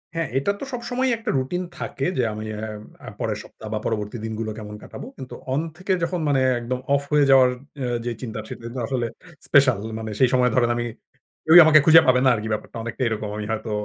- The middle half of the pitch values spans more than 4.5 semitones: Yes, average, 5.1 semitones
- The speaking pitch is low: Yes, low, 125 Hz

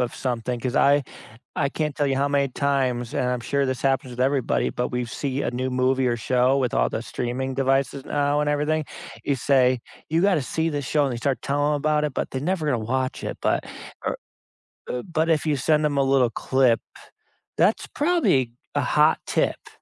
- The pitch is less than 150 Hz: Yes, low, 135 Hz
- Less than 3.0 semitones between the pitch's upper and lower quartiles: Yes, narrow, 2.6 semitones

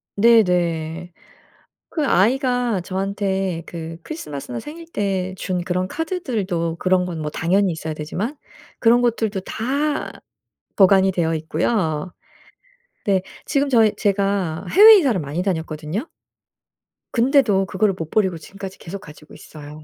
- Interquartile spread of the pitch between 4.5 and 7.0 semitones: Yes, wide, 5.4 semitones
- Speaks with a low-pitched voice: No, high, 190 Hz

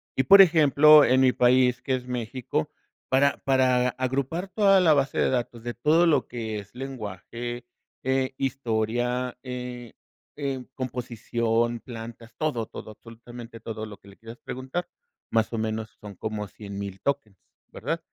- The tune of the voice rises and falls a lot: No, average, 2.8 semitones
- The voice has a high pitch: No, low, 125 Hz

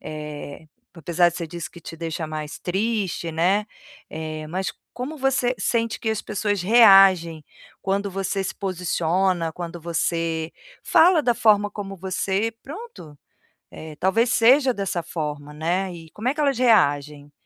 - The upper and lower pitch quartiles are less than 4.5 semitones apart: No, average, 4.8 semitones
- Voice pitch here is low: No, medium, 185 Hz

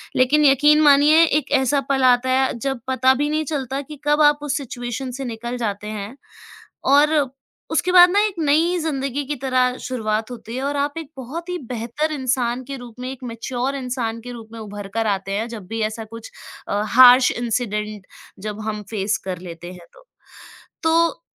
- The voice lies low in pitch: No, very high, 255 Hz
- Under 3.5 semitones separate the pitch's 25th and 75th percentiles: No, average, 4.3 semitones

